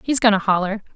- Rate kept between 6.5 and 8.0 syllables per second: Yes, 6.6 syllables/s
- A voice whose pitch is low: No, high, 205 Hz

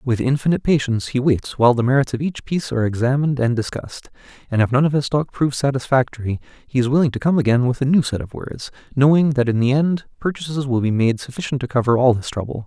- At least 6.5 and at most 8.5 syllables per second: Yes, 6.7 syllables/s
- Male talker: Yes, male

